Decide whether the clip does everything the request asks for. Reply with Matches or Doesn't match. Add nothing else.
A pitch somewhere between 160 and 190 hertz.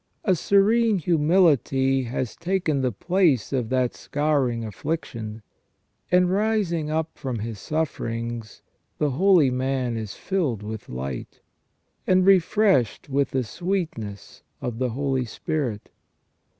Doesn't match